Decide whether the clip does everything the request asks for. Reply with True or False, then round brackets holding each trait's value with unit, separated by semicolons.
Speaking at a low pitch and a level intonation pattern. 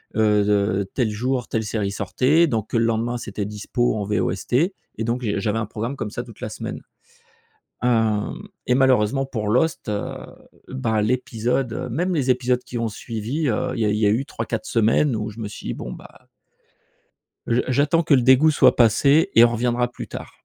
False (115 Hz; 3.2 semitones)